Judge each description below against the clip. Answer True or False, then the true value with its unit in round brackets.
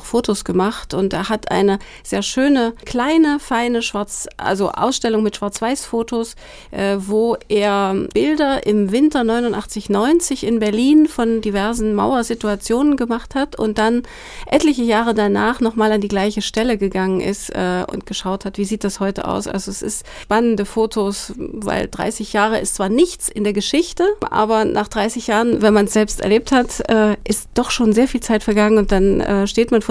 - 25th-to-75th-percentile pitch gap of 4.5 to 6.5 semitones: False (2.7 semitones)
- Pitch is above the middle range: True (220 Hz)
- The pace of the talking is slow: False (180 wpm)